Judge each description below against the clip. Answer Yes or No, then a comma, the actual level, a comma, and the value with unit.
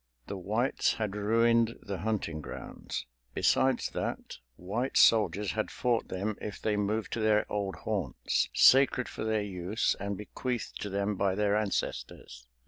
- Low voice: Yes, low, 105 Hz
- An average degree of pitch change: No, narrow, 2.1 semitones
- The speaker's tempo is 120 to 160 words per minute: Yes, average, 150 wpm